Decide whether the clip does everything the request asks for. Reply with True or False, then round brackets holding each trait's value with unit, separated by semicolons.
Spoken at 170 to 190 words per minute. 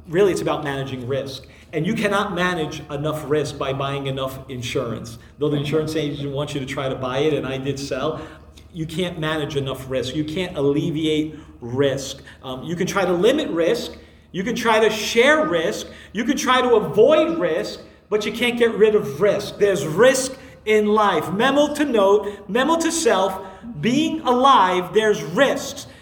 True (180 wpm)